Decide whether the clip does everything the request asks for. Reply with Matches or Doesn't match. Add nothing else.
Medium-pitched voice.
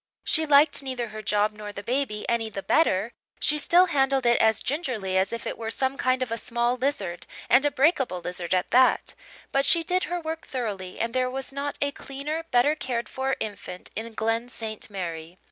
Doesn't match